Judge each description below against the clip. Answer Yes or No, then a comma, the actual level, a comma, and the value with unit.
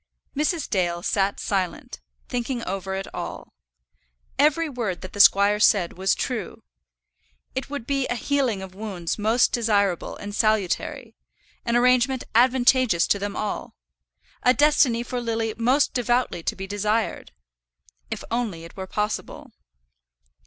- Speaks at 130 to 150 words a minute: Yes, average, 140 wpm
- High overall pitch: Yes, high, 220 Hz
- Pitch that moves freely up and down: No, average, 4.3 semitones